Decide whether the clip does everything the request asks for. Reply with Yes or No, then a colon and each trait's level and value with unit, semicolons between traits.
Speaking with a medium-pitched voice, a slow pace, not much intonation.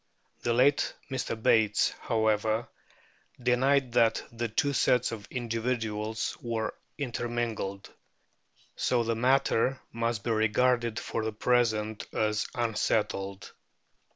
No: low, 115 Hz; slow, 105 wpm; narrow, 2.0 semitones